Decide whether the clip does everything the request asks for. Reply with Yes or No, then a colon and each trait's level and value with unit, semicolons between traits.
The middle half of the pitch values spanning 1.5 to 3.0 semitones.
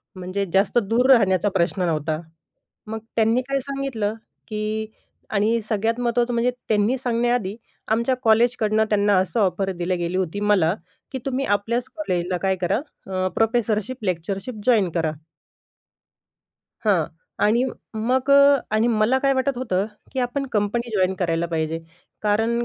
No: average, 4.2 semitones